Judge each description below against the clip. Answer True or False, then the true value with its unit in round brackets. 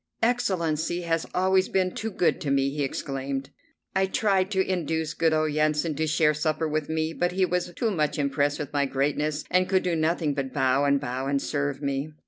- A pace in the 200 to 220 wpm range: True (205 wpm)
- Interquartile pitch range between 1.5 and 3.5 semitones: False (4.0 semitones)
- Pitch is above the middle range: False (155 Hz)